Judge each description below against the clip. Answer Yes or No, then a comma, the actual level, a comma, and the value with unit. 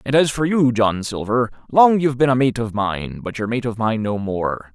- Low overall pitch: Yes, low, 120 Hz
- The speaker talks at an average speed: No, fast, 255 wpm